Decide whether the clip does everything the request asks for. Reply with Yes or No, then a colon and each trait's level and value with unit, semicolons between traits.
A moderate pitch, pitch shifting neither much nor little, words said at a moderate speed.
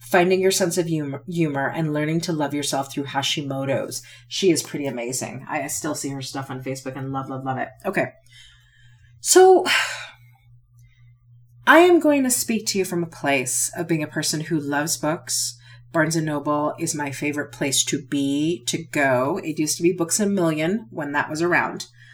Yes: medium, 145 Hz; average, 4.2 semitones; average, 190 wpm